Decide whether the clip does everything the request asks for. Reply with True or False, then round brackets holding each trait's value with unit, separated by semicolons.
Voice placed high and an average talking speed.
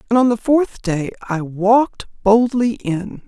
True (220 Hz; 165 wpm)